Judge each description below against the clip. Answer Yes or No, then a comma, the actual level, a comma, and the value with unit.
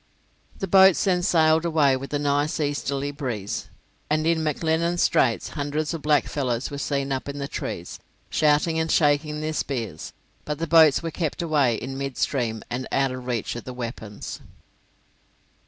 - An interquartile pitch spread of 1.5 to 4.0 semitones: Yes, average, 3.2 semitones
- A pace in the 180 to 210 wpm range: No, average, 165 wpm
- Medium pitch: Yes, medium, 145 Hz